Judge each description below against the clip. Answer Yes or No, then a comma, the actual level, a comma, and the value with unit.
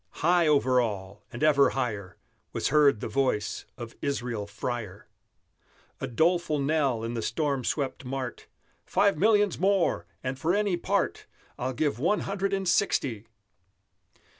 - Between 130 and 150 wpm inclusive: Yes, average, 140 wpm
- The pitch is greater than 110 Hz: Yes, low, 135 Hz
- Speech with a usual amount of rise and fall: No, wide, 6.3 semitones